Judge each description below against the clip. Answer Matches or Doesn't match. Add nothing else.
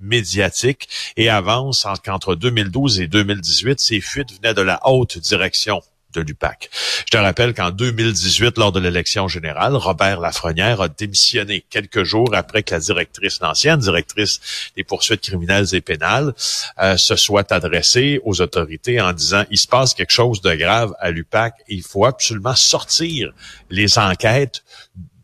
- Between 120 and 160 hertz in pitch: Doesn't match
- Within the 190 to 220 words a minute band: Doesn't match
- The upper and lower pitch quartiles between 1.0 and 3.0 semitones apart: Doesn't match